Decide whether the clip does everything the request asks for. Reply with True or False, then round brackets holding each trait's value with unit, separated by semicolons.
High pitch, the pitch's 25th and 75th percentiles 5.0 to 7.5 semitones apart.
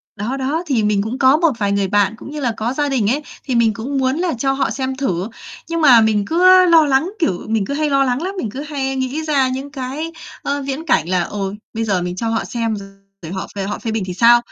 True (255 Hz; 5.4 semitones)